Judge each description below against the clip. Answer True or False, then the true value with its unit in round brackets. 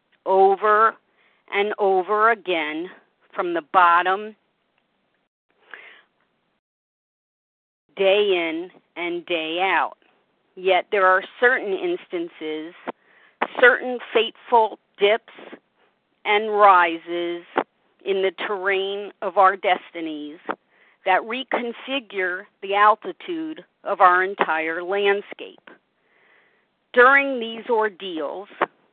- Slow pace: True (80 wpm)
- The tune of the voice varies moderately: True (3.7 semitones)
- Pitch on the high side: True (200 Hz)